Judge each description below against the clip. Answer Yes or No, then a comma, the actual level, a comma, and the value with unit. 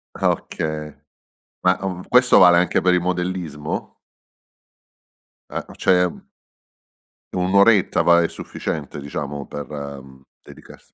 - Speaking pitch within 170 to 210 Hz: No, very low, 85 Hz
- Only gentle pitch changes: No, average, 4.0 semitones